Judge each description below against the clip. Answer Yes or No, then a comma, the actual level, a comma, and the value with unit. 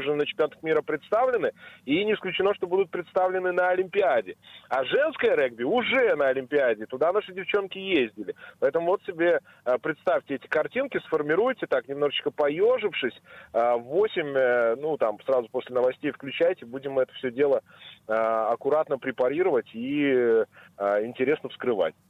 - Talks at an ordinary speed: Yes, average, 140 wpm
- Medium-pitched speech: Yes, medium, 155 Hz